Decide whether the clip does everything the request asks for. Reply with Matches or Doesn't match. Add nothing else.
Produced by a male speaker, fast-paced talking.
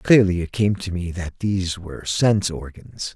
Doesn't match